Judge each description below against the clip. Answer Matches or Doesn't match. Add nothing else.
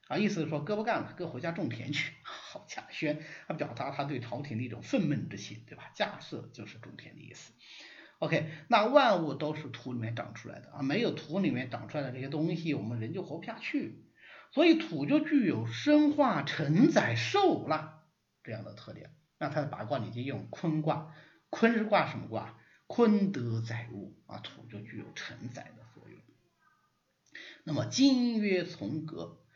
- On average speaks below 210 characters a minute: Doesn't match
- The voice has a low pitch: Doesn't match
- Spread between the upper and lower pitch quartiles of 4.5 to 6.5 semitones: Doesn't match